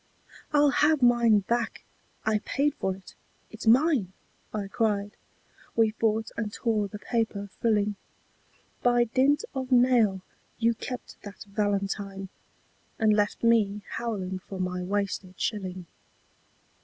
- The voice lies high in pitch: Yes, high, 215 Hz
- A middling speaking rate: No, slow, 130 wpm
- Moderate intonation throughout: Yes, average, 3.0 semitones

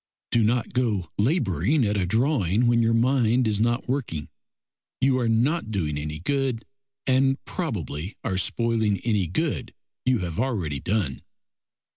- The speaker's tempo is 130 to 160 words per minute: Yes, average, 145 wpm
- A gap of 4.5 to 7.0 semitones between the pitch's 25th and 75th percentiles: Yes, wide, 5.5 semitones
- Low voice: Yes, low, 115 Hz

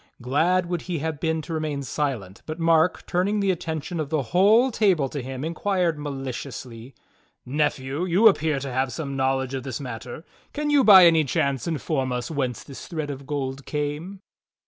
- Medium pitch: Yes, medium, 150 Hz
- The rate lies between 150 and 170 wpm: No, average, 180 wpm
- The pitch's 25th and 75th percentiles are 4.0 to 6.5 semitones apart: Yes, average, 4.3 semitones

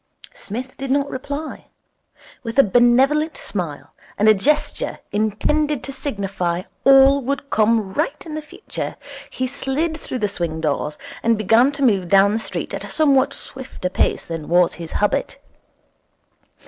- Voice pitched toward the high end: Yes, high, 245 Hz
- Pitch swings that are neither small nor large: No, wide, 6.0 semitones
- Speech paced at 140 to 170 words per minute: Yes, average, 155 wpm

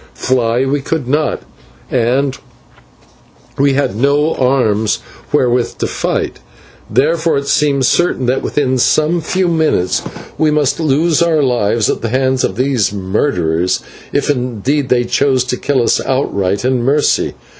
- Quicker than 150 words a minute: No, average, 145 wpm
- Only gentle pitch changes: No, average, 3.3 semitones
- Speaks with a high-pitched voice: No, low, 130 Hz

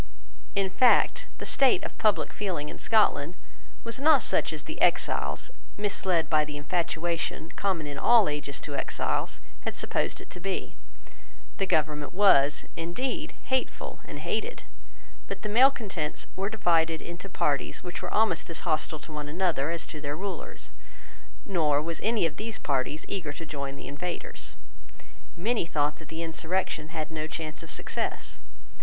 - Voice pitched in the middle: Yes, medium, 165 Hz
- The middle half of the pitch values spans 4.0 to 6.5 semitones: Yes, average, 4.6 semitones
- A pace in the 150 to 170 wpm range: Yes, average, 160 wpm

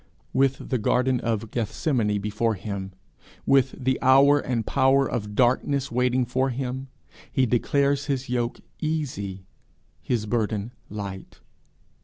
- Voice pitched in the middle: No, low, 125 Hz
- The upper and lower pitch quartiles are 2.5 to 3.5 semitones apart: No, average, 3.9 semitones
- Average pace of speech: No, slow, 130 wpm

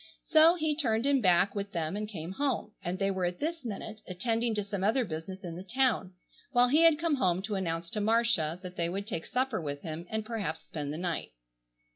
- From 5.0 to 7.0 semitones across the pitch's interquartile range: Yes, wide, 5.6 semitones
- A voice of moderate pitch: No, high, 200 Hz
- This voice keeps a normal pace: No, fast, 225 wpm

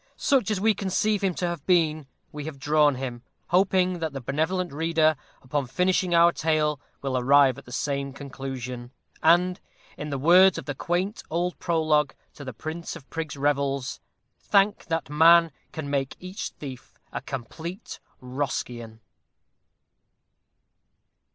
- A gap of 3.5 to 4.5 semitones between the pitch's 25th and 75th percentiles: Yes, average, 4.2 semitones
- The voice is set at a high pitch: No, medium, 155 Hz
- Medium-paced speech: Yes, average, 145 wpm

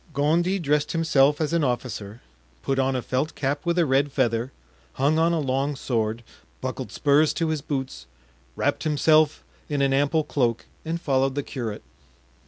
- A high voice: No, medium, 140 Hz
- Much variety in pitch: No, average, 3.0 semitones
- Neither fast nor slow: Yes, average, 170 wpm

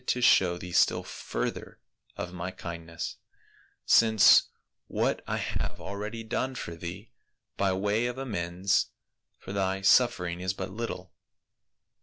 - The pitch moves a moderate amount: Yes, average, 4.0 semitones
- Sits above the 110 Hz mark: No, very low, 95 Hz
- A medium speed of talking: No, slow, 130 wpm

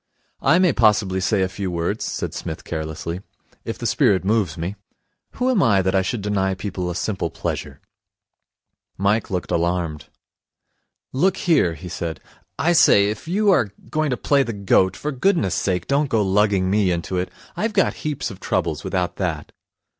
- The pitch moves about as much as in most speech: No, wide, 6.2 semitones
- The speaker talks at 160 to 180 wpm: Yes, average, 175 wpm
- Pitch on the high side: No, low, 100 Hz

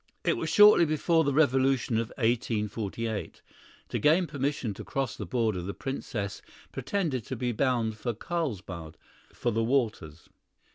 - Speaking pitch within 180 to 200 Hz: No, low, 120 Hz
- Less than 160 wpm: Yes, average, 145 wpm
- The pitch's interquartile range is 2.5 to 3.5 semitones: No, average, 4.5 semitones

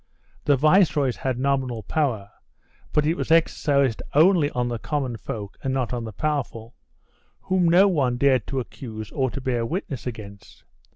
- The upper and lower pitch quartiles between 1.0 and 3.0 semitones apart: No, average, 4.2 semitones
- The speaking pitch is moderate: No, low, 130 Hz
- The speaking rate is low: No, average, 165 wpm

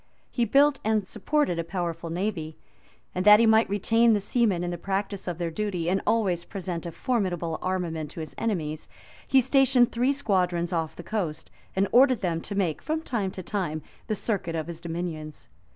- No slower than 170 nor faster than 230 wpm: Yes, average, 190 wpm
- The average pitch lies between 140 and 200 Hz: Yes, high, 190 Hz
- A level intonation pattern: No, average, 4.7 semitones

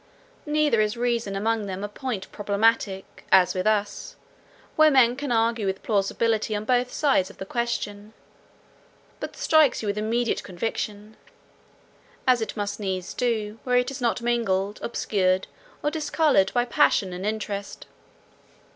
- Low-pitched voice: No, high, 220 Hz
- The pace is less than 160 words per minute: Yes, average, 145 wpm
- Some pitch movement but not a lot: Yes, average, 3.2 semitones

